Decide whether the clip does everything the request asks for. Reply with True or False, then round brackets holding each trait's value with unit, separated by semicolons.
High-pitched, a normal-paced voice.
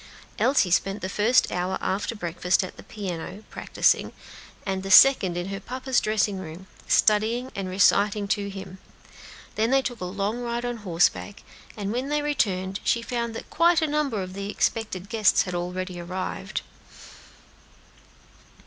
True (200 Hz; 160 wpm)